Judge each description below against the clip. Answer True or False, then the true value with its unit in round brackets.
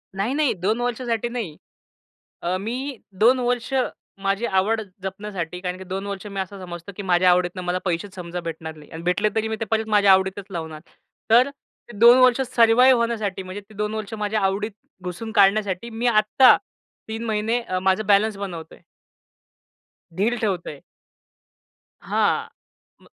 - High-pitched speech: True (205 Hz)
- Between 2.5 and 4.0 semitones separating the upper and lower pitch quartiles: True (3.5 semitones)